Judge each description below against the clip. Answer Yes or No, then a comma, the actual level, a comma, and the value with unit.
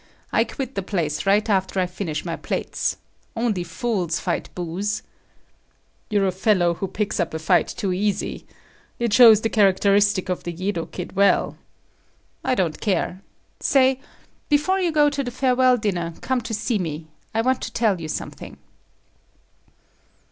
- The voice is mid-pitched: No, high, 200 Hz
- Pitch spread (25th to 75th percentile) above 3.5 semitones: Yes, average, 4.7 semitones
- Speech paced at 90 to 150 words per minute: No, average, 160 wpm